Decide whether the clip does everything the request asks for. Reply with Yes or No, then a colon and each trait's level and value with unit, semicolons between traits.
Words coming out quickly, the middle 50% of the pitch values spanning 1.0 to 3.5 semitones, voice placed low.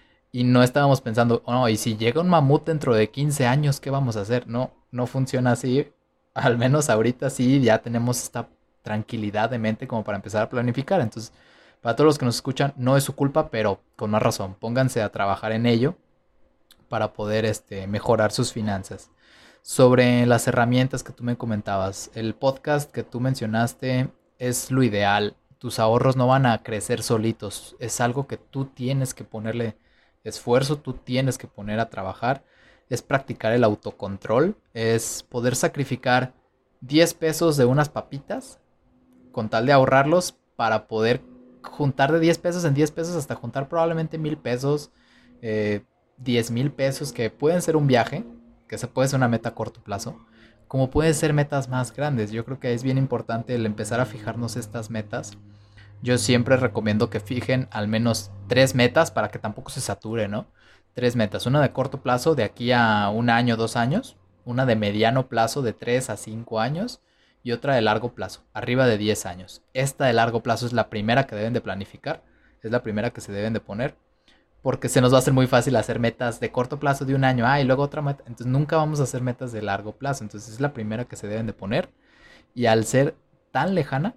Yes: fast, 195 wpm; average, 3.2 semitones; low, 120 Hz